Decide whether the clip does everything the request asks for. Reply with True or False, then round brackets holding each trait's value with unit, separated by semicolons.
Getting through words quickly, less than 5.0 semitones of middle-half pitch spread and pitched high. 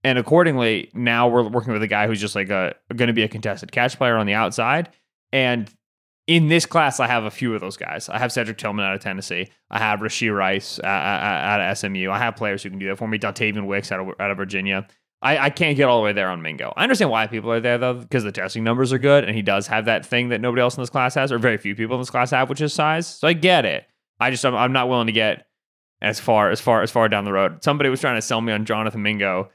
False (280 wpm; 3.6 semitones; 115 Hz)